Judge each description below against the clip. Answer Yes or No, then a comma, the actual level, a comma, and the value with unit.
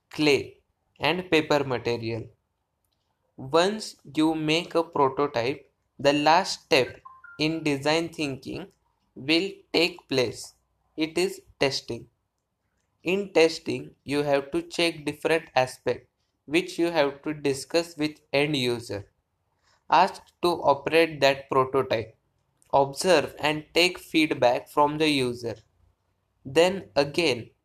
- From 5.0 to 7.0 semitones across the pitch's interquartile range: Yes, wide, 5.4 semitones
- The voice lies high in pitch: No, medium, 145 Hz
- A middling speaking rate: No, slow, 110 wpm